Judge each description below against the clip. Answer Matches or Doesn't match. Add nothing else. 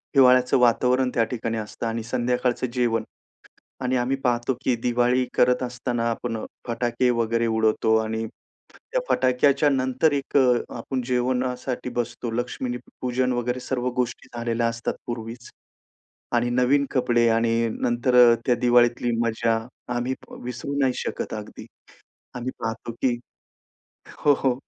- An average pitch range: Doesn't match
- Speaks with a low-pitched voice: Matches